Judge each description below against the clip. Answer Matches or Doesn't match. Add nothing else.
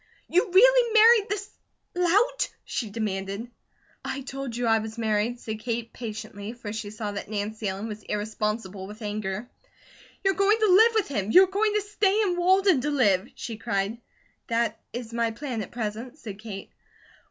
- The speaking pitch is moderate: Doesn't match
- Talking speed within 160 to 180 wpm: Matches